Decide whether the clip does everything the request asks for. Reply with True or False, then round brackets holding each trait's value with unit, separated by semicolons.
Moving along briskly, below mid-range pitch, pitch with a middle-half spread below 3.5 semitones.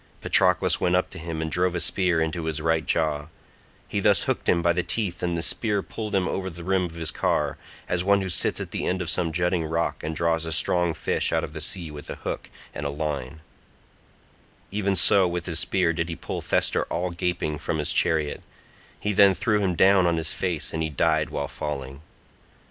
True (220 wpm; 85 Hz; 2.5 semitones)